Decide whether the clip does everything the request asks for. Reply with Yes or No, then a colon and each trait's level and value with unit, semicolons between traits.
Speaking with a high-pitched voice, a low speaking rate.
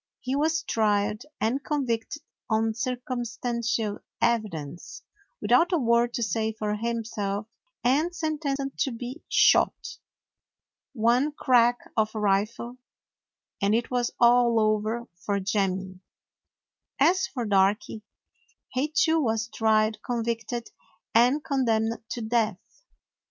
Yes: high, 235 Hz; slow, 115 wpm